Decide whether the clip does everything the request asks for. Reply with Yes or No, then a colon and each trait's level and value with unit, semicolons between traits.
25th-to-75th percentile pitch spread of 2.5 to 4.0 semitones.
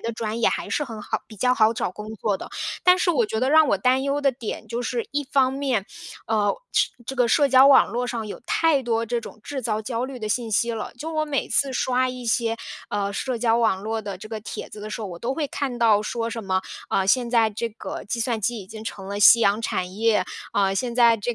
Yes: average, 3.1 semitones